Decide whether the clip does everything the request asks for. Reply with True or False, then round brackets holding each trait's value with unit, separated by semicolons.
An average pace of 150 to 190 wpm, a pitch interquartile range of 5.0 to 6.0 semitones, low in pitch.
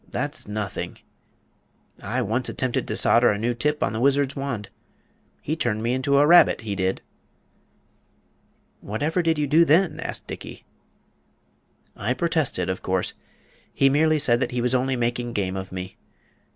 True (160 wpm; 5.6 semitones; 125 Hz)